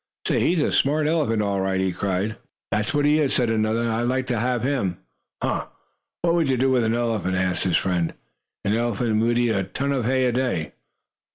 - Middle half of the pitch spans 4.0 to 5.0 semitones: Yes, average, 4.7 semitones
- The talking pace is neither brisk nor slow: No, fast, 215 wpm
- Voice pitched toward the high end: No, low, 115 Hz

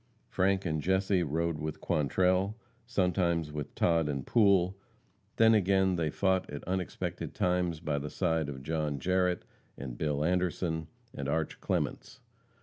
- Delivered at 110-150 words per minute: Yes, average, 145 wpm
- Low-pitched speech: Yes, very low, 85 Hz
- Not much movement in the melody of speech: No, average, 3.7 semitones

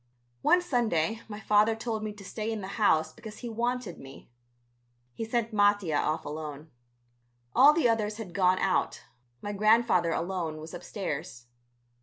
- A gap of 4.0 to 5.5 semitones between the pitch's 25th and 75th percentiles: Yes, average, 5.2 semitones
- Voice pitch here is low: No, high, 205 Hz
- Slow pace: No, average, 155 wpm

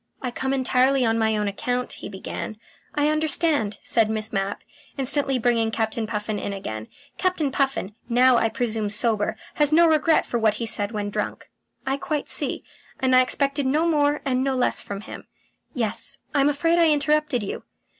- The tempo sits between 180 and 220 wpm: Yes, average, 185 wpm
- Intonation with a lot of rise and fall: No, average, 4.9 semitones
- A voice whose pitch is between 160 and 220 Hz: No, very high, 255 Hz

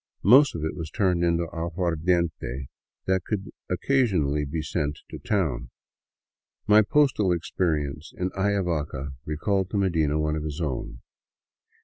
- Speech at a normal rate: No, slow, 130 wpm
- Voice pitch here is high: No, very low, 85 Hz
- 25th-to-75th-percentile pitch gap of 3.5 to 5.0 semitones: Yes, average, 4.2 semitones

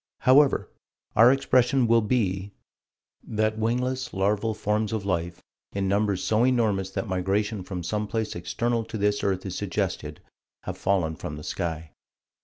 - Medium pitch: No, low, 105 Hz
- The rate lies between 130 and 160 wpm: Yes, average, 150 wpm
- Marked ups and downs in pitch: No, average, 3.4 semitones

